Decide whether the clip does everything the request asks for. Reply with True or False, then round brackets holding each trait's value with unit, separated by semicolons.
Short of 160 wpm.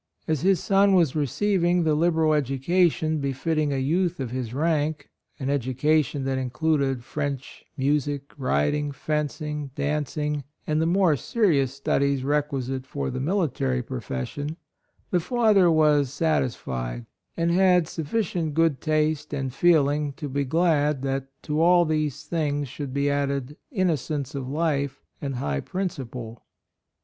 True (140 wpm)